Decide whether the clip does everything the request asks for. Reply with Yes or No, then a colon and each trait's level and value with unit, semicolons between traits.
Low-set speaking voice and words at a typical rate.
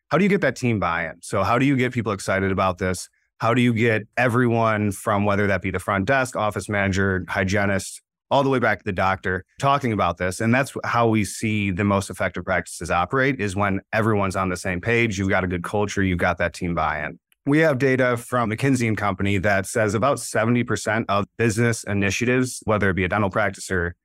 No: low, 105 Hz; fast, 220 wpm